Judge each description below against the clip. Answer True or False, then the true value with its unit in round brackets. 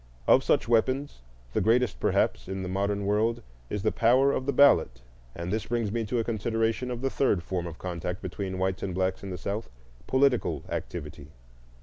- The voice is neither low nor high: False (105 Hz)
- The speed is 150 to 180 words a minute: False (190 wpm)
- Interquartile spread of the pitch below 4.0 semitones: False (4.3 semitones)